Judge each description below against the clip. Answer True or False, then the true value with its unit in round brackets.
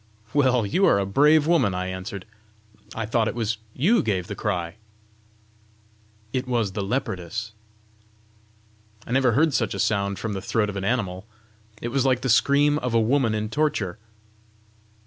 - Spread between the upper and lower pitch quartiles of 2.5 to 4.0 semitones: False (4.9 semitones)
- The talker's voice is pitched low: True (115 Hz)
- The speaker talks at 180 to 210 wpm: False (165 wpm)